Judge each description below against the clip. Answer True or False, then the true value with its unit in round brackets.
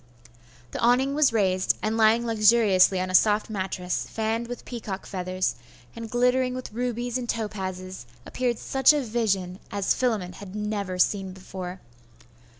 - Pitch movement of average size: True (4.2 semitones)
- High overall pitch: True (215 Hz)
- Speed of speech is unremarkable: True (150 wpm)